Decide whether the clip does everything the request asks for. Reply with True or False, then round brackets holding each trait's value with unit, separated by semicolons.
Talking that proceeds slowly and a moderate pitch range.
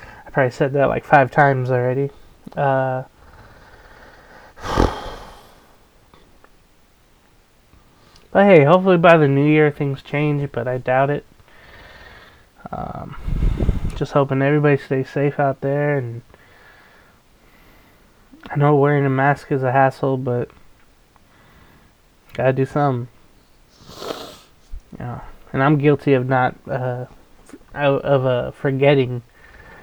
False (105 wpm; 2.1 semitones)